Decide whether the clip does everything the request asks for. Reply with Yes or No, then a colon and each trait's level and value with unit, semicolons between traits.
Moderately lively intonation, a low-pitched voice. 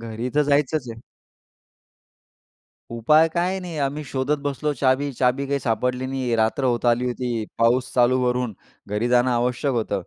Yes: average, 3.0 semitones; low, 125 Hz